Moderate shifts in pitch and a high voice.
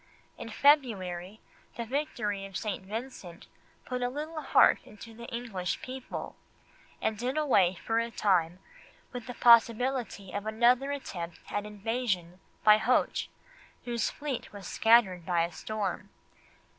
Yes: average, 4.3 semitones; high, 225 Hz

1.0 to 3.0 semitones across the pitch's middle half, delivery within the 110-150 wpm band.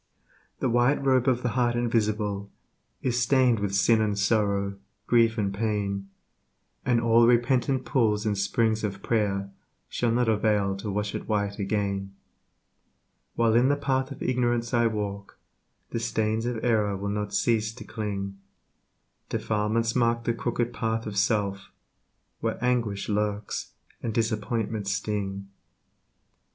Yes: average, 2.7 semitones; average, 140 wpm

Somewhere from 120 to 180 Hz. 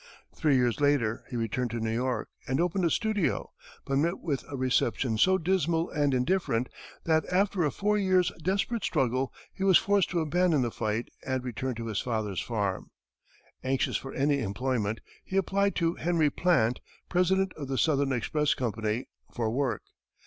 Yes: medium, 140 Hz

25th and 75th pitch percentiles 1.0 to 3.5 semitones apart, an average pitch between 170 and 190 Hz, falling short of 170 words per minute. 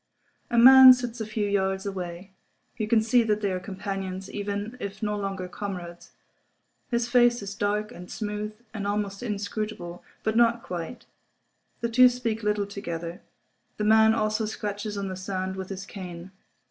No: narrow, 2.5 semitones; high, 205 Hz; average, 160 wpm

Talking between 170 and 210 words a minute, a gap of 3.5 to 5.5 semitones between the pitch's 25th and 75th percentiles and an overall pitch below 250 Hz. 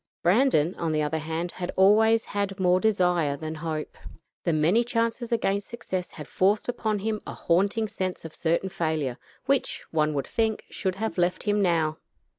Yes: average, 175 wpm; average, 5.1 semitones; medium, 185 Hz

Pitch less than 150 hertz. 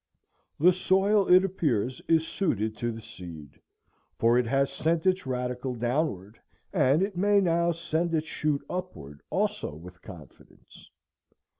Yes: medium, 140 Hz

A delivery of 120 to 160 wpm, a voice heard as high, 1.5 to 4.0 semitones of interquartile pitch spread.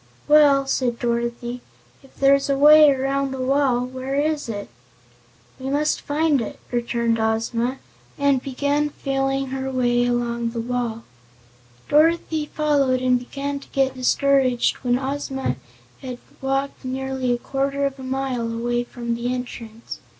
Yes: average, 145 wpm; very high, 265 Hz; narrow, 2.4 semitones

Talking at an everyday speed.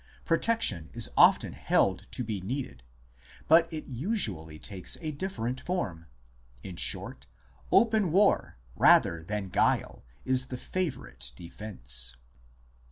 No: slow, 115 wpm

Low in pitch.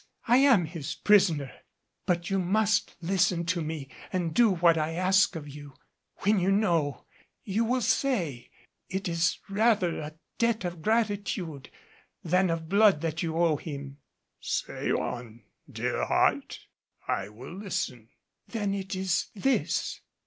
No: medium, 175 Hz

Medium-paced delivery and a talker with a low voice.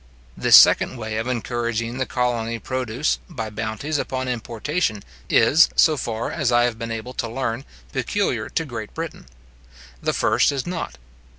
Yes: average, 160 wpm; low, 120 Hz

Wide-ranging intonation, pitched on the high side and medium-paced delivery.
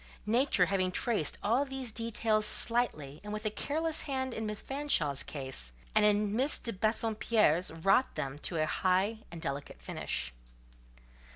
Yes: wide, 6.1 semitones; high, 210 Hz; average, 155 wpm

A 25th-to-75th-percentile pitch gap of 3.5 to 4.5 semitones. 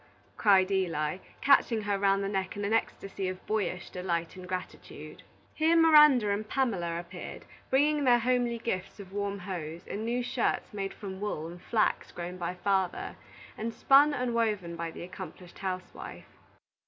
Yes: average, 4.2 semitones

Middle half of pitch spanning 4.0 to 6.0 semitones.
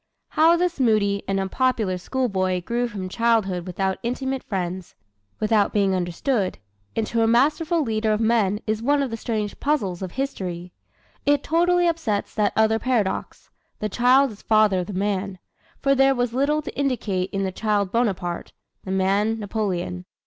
Yes: average, 5.1 semitones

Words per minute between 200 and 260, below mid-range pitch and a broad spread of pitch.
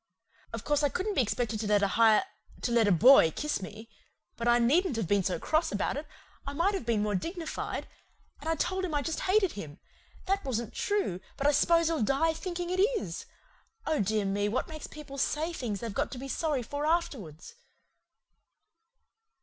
No: fast, 205 wpm; very high, 275 Hz; wide, 7.5 semitones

